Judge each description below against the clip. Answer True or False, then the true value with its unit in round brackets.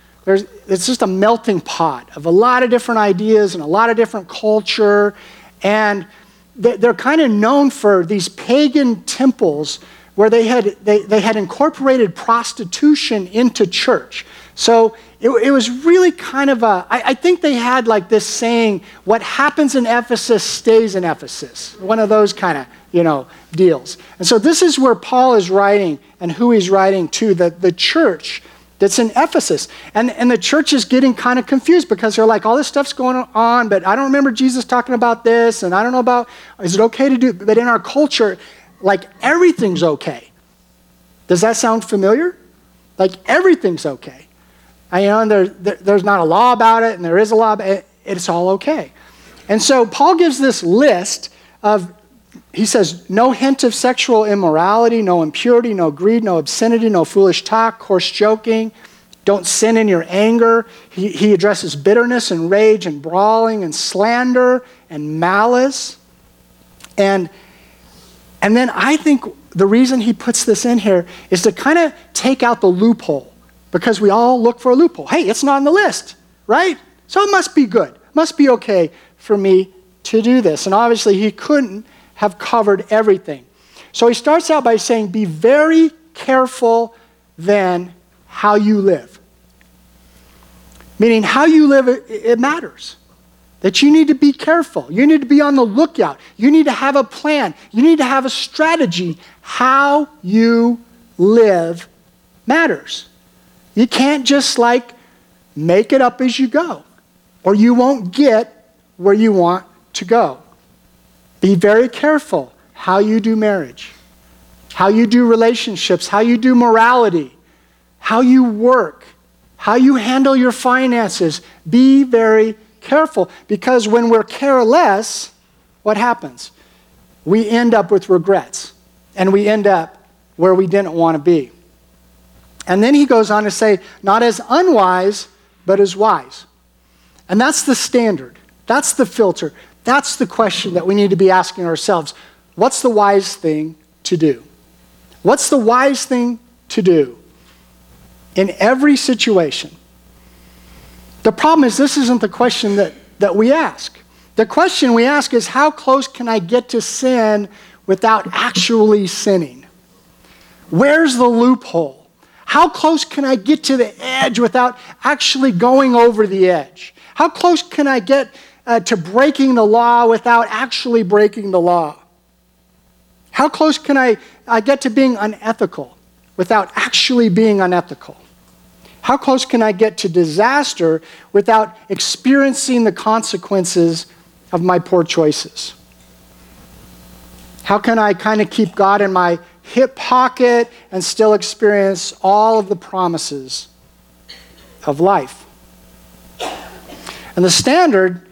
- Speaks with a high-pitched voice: True (215 Hz)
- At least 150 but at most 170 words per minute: True (160 wpm)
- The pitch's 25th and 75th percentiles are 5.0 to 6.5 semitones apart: True (5.5 semitones)